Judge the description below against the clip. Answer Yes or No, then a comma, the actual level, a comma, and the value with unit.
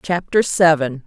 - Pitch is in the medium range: Yes, medium, 160 Hz